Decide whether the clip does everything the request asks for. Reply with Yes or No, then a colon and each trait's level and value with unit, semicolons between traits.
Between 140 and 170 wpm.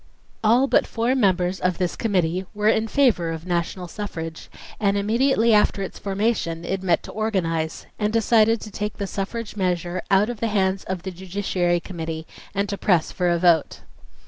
No: average, 180 wpm